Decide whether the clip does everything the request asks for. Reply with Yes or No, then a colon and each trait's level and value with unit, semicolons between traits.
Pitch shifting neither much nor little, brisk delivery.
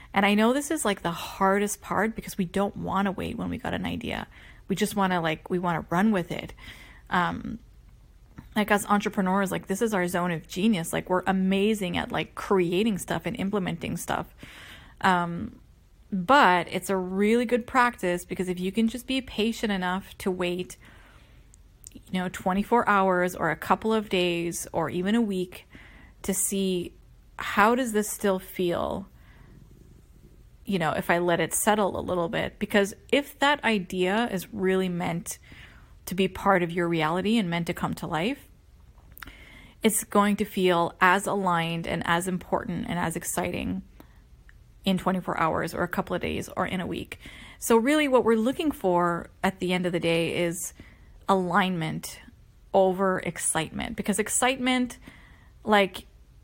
No: average, 3.0 semitones; average, 170 wpm